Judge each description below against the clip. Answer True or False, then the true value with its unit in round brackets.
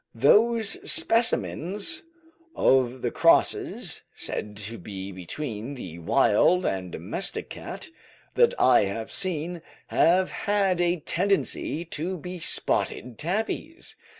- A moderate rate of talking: False (110 wpm)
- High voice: False (165 Hz)